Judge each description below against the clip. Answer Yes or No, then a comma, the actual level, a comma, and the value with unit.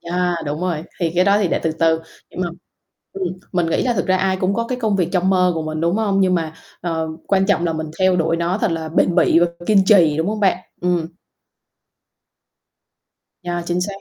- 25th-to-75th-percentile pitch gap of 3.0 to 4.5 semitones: No, narrow, 2.6 semitones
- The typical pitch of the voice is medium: Yes, medium, 180 Hz